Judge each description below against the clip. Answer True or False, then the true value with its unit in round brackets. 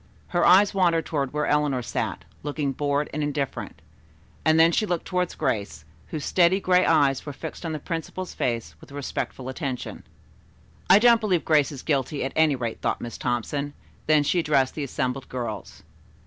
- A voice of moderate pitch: True (150 Hz)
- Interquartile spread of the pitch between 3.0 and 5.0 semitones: True (3.6 semitones)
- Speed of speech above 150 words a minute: True (175 wpm)